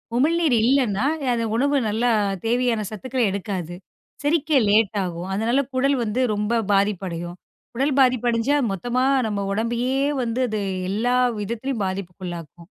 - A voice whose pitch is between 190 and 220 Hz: No, high, 230 Hz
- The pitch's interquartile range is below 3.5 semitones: No, average, 4.4 semitones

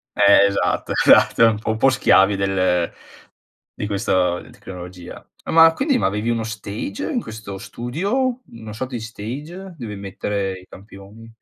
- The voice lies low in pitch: Yes, low, 110 Hz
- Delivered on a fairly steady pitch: No, average, 4.4 semitones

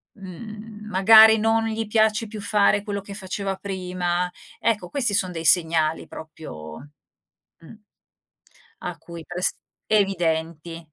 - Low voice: No, high, 190 Hz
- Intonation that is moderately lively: Yes, average, 4.0 semitones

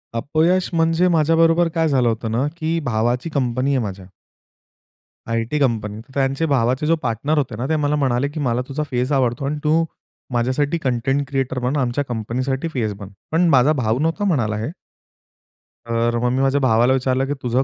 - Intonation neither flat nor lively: Yes, average, 4.1 semitones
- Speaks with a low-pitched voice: Yes, low, 130 Hz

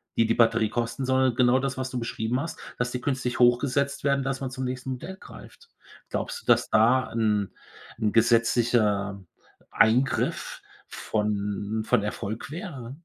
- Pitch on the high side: No, low, 120 Hz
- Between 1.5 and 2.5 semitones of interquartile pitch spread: No, average, 2.9 semitones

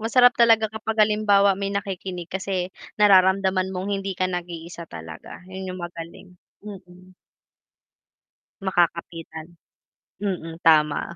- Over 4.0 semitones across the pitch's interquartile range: No, narrow, 2.5 semitones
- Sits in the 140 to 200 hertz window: Yes, medium, 185 Hz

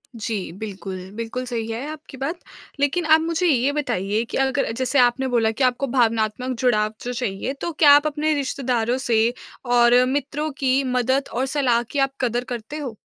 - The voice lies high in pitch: Yes, very high, 255 Hz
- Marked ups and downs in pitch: No, average, 3.5 semitones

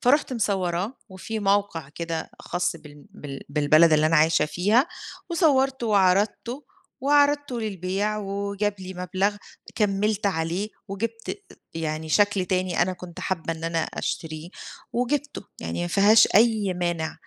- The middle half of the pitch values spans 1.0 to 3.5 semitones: No, average, 4.6 semitones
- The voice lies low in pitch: No, high, 190 Hz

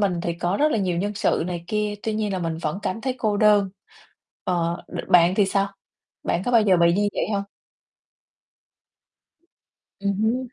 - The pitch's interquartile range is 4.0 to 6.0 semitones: No, average, 3.2 semitones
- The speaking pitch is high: Yes, high, 200 Hz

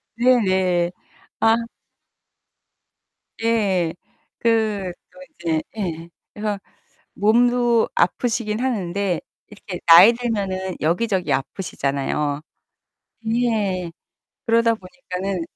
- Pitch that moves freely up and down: No, average, 4.5 semitones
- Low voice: No, high, 195 Hz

